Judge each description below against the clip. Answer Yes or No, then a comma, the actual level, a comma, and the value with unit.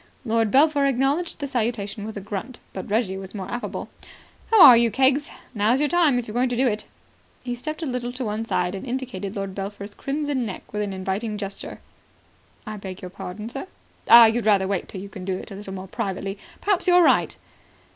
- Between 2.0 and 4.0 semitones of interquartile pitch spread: No, average, 4.8 semitones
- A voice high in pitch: Yes, high, 220 Hz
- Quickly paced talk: Yes, fast, 215 wpm